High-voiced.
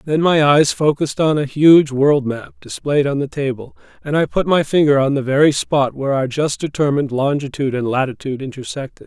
No: medium, 140 Hz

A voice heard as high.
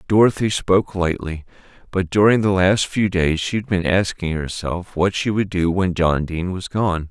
No: very low, 95 Hz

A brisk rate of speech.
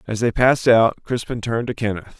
Yes: fast, 220 wpm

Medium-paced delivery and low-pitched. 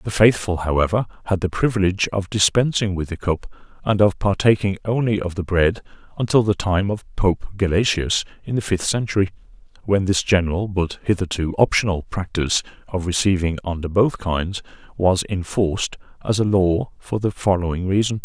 Yes: average, 160 wpm; very low, 95 Hz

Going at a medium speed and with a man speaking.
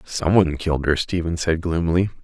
Yes: average, 160 wpm; male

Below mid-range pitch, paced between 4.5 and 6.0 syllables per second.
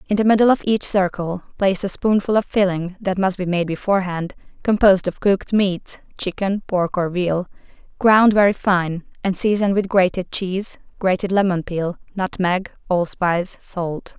No: high, 190 Hz; 4.8 syllables/s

